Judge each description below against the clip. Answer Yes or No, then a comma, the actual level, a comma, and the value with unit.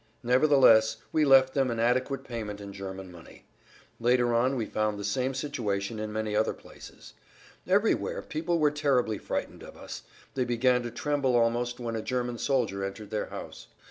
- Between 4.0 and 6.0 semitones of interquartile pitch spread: No, average, 3.5 semitones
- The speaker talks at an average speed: Yes, average, 175 wpm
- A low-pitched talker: Yes, low, 120 Hz